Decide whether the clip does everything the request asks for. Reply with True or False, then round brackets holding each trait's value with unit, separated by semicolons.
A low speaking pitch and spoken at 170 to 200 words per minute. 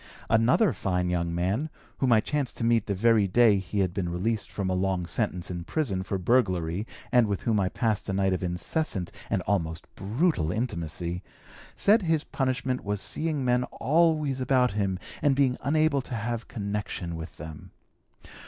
True (105 Hz; 175 wpm)